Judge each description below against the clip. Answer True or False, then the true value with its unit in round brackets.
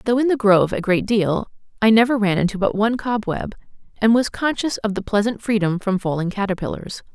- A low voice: False (210 Hz)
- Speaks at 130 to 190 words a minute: False (200 wpm)